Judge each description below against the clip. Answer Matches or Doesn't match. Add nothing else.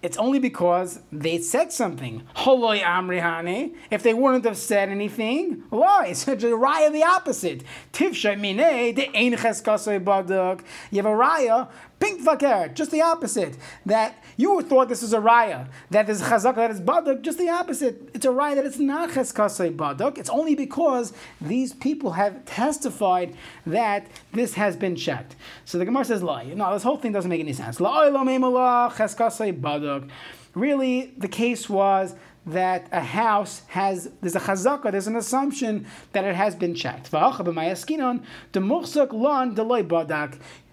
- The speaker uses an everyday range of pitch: Doesn't match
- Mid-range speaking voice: Doesn't match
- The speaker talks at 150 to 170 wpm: Matches